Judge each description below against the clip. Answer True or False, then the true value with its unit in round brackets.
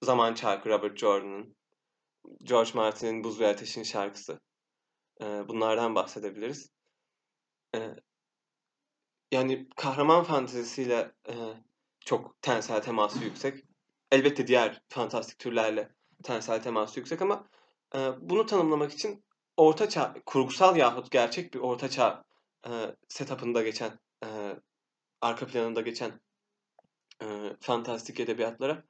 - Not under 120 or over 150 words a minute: False (95 wpm)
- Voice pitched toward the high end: False (120 Hz)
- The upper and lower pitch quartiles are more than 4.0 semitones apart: False (3.6 semitones)